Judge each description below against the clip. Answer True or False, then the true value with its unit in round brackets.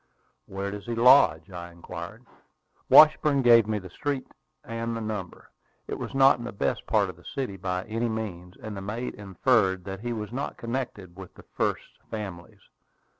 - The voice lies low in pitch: True (105 Hz)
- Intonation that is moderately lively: True (4.1 semitones)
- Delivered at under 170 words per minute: False (175 wpm)